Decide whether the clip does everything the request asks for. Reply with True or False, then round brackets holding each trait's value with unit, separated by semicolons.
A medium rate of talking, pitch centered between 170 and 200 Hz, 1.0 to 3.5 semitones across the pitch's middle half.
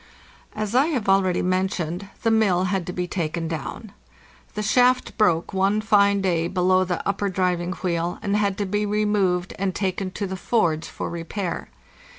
True (170 wpm; 190 Hz; 2.6 semitones)